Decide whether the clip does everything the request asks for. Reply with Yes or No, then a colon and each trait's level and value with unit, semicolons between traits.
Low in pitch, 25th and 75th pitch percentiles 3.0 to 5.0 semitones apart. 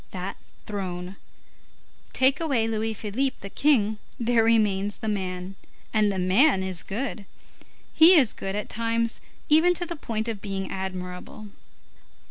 No: high, 215 Hz; average, 3.6 semitones